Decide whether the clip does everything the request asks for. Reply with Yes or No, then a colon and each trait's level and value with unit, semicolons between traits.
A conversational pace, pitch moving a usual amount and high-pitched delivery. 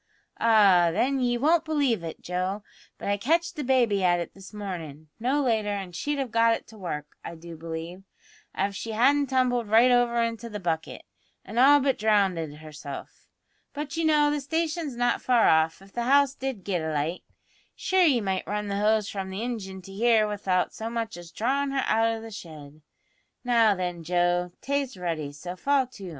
No: average, 195 wpm; wide, 6.1 semitones; high, 215 Hz